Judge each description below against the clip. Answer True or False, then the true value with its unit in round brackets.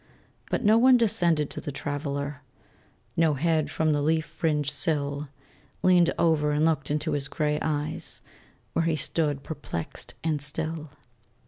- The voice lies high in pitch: False (150 Hz)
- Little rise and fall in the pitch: True (1.9 semitones)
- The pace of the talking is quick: False (145 wpm)